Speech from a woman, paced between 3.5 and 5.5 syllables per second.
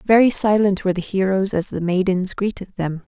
Yes: female; 5.4 syllables/s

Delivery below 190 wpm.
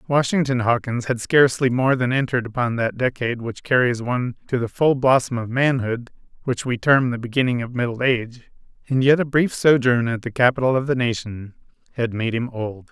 No: average, 195 wpm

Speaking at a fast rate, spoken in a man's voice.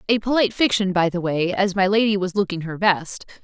No: fast, 225 wpm; female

